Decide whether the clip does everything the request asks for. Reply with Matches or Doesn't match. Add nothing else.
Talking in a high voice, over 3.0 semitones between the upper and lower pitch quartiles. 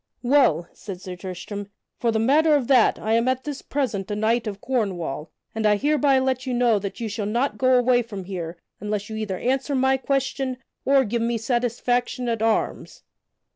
Matches